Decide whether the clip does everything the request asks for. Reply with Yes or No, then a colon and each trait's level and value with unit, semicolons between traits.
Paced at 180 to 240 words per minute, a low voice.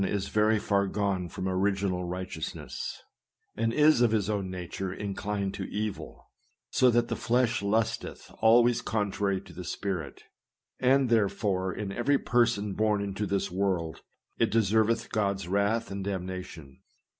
No: average, 145 wpm; low, 100 Hz